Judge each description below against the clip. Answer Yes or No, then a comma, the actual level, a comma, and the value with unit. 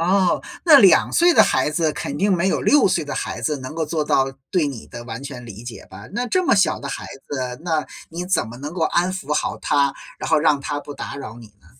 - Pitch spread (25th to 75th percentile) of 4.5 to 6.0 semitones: Yes, average, 5.1 semitones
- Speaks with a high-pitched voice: No, medium, 150 Hz